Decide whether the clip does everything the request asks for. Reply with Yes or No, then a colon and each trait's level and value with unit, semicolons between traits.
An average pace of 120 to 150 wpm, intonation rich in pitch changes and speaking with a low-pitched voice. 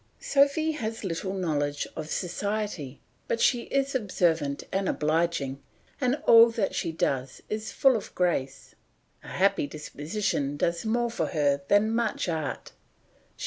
No: average, 140 wpm; wide, 7.1 semitones; medium, 185 Hz